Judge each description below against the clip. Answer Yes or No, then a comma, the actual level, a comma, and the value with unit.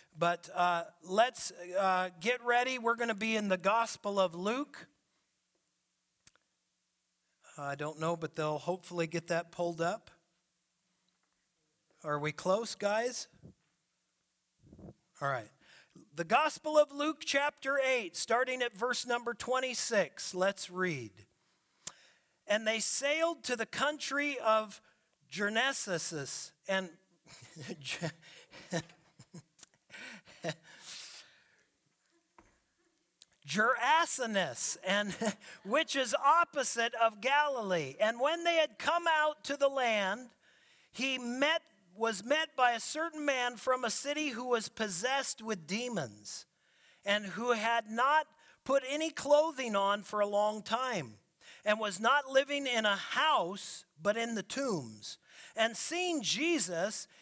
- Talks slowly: Yes, slow, 115 wpm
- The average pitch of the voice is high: Yes, high, 220 Hz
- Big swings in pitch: Yes, wide, 7.0 semitones